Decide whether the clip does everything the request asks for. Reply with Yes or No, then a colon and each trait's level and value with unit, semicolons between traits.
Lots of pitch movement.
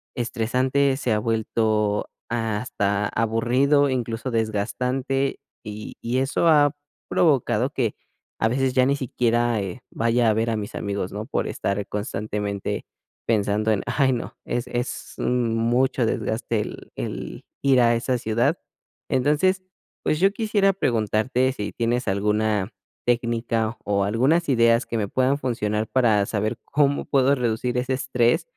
No: average, 3.3 semitones